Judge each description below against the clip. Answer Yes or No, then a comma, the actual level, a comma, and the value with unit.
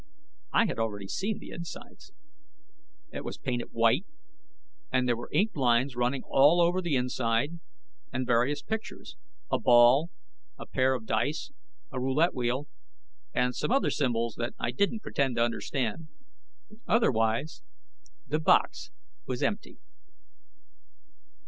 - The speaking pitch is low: Yes, low, 130 Hz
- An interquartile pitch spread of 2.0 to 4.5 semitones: No, average, 4.9 semitones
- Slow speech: Yes, slow, 130 wpm